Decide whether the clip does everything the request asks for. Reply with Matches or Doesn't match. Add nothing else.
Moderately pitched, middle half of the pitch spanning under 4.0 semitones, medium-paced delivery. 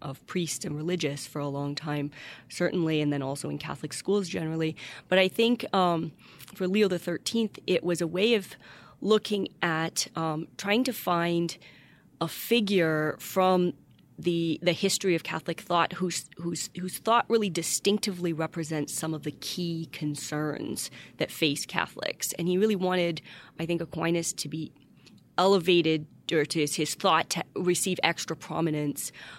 Matches